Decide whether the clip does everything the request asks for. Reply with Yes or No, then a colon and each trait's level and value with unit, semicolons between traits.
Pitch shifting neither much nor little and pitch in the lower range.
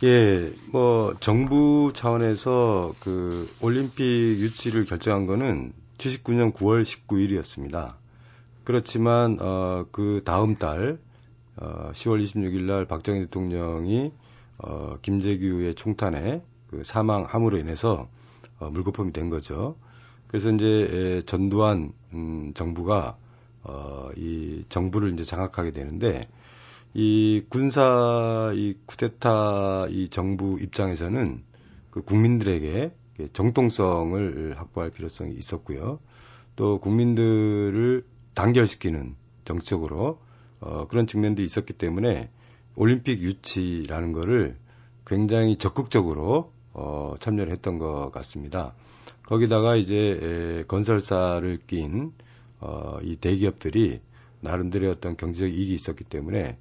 Yes: average, 4.9 semitones; low, 105 Hz